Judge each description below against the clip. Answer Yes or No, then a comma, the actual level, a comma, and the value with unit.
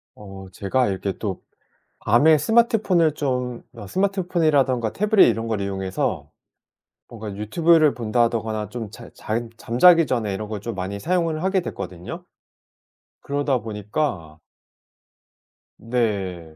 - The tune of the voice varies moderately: No, wide, 7.3 semitones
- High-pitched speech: No, low, 115 Hz